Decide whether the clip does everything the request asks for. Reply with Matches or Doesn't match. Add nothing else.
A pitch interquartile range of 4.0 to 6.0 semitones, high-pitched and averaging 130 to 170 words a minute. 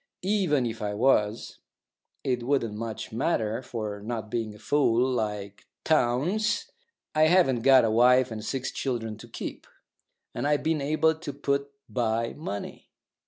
Doesn't match